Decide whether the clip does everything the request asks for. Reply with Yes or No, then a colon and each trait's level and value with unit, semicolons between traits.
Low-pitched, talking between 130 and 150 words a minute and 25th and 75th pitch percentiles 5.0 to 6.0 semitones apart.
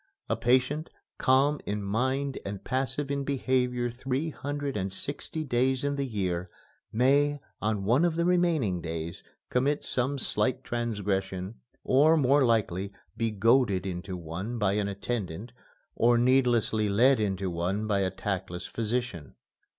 Yes: low, 120 Hz; average, 145 wpm; wide, 5.4 semitones